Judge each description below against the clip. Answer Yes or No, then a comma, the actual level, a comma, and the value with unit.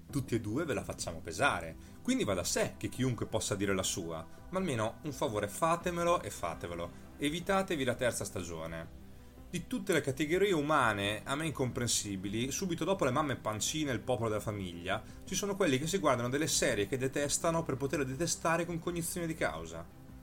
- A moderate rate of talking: No, fast, 185 wpm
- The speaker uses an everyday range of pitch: No, wide, 8.4 semitones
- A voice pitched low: Yes, low, 130 Hz